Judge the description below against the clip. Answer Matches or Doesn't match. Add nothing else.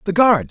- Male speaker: Matches